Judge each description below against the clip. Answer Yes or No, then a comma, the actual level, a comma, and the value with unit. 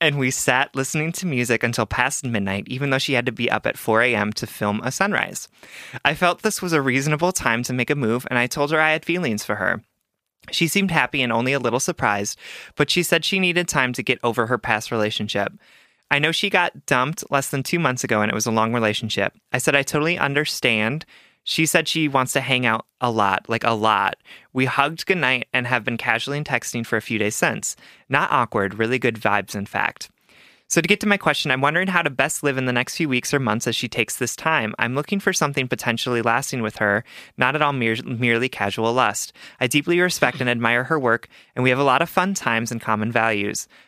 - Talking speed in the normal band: No, fast, 235 wpm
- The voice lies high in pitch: No, low, 125 Hz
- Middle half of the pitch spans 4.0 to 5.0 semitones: Yes, average, 4.5 semitones